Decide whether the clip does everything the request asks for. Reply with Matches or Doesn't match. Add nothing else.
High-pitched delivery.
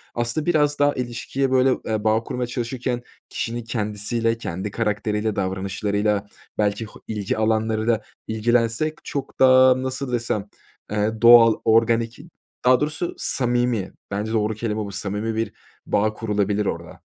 Doesn't match